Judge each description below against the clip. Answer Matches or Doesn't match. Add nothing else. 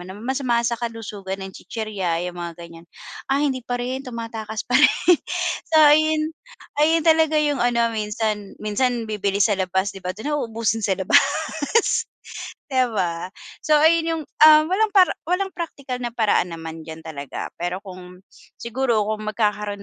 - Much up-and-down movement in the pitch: Matches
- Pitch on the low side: Doesn't match